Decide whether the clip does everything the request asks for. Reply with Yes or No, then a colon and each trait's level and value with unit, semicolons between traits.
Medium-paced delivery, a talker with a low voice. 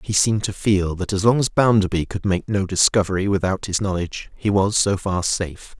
No: fast, 220 wpm; low, 100 Hz